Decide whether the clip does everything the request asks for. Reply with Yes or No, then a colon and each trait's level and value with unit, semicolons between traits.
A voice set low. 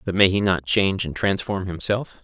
Yes: very low, 95 Hz